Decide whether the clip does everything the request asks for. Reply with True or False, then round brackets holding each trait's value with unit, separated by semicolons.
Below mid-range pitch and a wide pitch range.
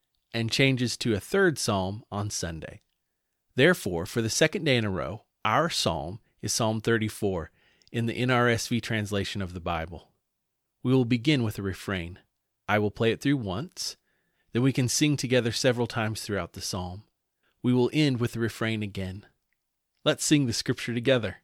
False (115 Hz; 4.0 semitones)